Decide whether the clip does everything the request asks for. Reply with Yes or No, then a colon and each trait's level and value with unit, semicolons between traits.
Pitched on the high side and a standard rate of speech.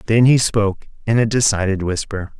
No: low, 105 Hz; average, 175 wpm